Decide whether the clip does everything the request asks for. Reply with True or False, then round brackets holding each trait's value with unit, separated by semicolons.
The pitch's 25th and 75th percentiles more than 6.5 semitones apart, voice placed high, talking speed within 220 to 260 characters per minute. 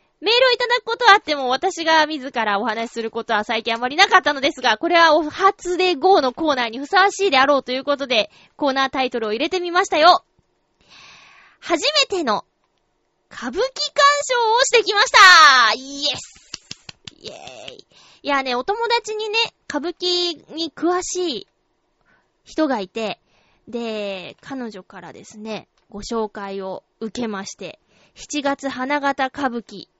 False (7.3 semitones; 290 Hz; 300 characters per minute)